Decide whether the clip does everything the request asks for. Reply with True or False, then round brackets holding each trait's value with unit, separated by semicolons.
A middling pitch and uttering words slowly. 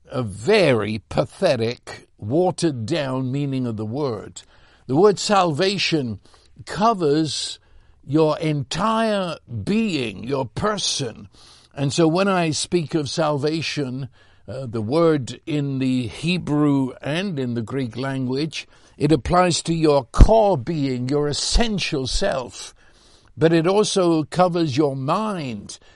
True (150 Hz; 120 wpm)